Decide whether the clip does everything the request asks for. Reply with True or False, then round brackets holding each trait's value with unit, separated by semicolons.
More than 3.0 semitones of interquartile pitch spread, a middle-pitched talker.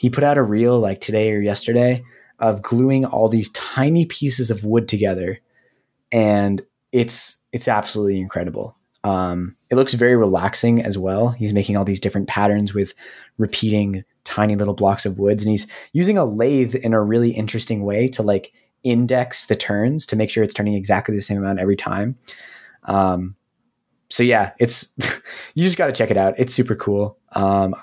False (3.4 semitones; 110 Hz)